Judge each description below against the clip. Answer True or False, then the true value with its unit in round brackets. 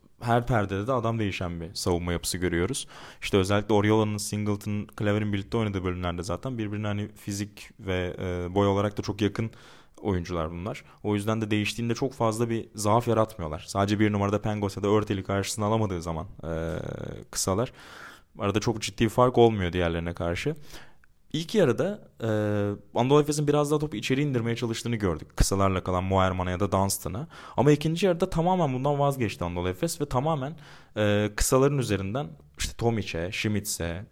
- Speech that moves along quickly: True (160 wpm)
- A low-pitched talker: True (105 Hz)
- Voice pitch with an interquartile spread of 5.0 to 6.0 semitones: False (3.7 semitones)